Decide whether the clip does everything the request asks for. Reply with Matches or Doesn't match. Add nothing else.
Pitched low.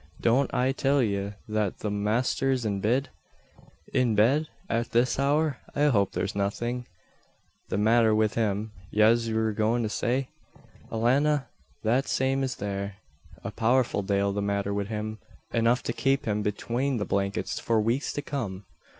Matches